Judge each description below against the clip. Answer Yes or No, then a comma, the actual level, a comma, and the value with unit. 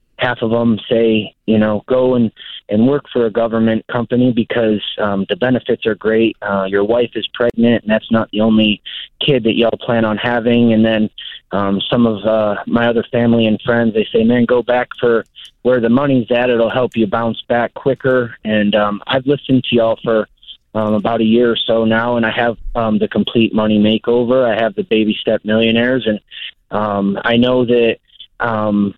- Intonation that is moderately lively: No, narrow, 1.9 semitones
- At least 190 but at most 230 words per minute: Yes, average, 200 wpm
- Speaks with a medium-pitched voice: No, low, 115 Hz